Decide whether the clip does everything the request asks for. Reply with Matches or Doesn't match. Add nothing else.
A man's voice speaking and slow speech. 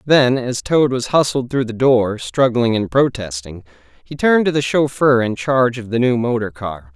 Doesn't match